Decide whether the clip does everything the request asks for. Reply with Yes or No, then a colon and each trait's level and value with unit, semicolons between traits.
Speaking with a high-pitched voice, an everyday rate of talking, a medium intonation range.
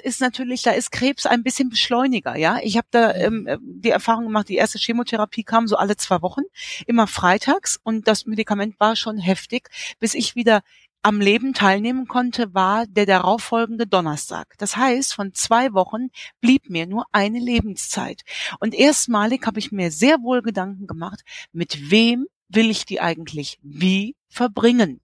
Yes: high, 225 Hz; average, 170 wpm; average, 3.3 semitones